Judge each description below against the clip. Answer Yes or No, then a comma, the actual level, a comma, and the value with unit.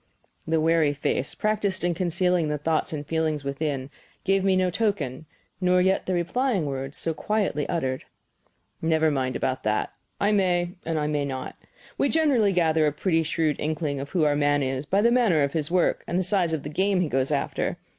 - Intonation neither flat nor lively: Yes, average, 4.3 semitones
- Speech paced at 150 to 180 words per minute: No, average, 200 wpm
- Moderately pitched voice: Yes, medium, 160 Hz